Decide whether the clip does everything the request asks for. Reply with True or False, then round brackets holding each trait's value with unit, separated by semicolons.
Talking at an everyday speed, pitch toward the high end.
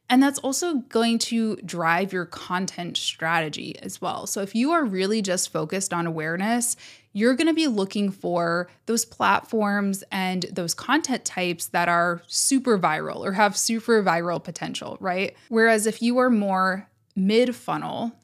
True (160 wpm; 205 Hz)